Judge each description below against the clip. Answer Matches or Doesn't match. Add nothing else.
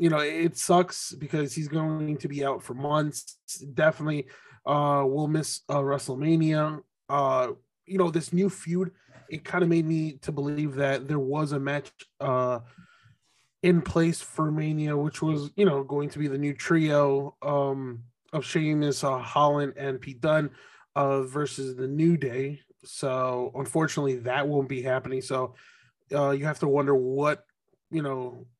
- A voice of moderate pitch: Matches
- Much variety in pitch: Doesn't match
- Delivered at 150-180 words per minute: Matches